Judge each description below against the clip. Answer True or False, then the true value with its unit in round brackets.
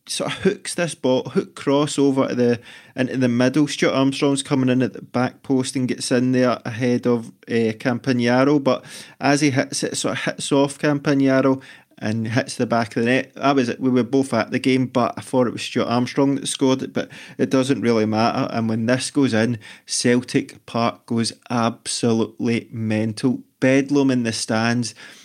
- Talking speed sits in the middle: True (195 wpm)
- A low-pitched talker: True (130 Hz)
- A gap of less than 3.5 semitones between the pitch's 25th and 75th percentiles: True (2.7 semitones)